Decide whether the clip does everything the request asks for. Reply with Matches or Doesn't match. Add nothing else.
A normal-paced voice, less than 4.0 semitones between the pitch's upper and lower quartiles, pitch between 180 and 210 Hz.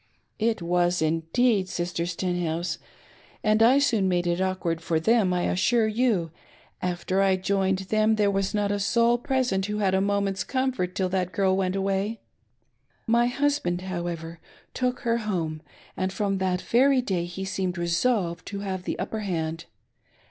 Matches